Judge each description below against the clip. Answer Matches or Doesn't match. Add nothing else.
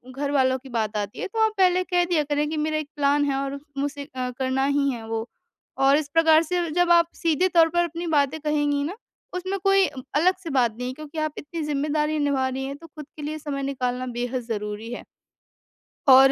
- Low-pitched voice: Doesn't match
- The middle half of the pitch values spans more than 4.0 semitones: Doesn't match